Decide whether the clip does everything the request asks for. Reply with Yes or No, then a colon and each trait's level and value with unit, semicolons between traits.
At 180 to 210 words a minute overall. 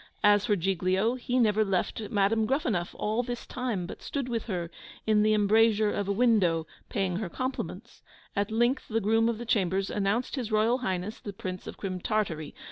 Yes: average, 190 wpm